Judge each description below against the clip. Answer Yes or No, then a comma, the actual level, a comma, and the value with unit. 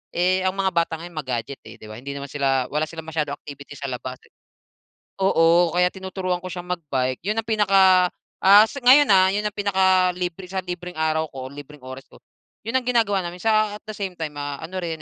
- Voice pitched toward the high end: No, medium, 180 Hz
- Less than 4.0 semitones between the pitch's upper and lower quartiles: No, average, 4.7 semitones